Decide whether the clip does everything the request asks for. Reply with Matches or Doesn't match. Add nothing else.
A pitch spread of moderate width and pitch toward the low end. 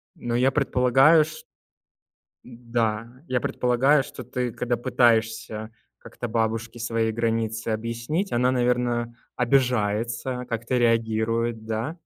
Doesn't match